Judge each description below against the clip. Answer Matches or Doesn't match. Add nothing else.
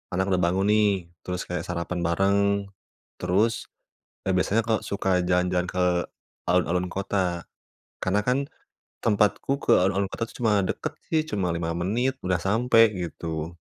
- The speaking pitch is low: Matches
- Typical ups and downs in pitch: Matches